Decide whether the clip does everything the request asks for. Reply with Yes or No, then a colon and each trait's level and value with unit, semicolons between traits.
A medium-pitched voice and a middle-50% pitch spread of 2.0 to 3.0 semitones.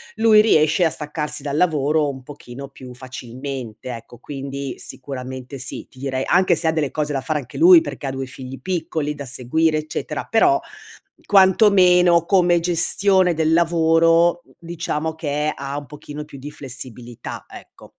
No: medium, 150 Hz; average, 4.2 semitones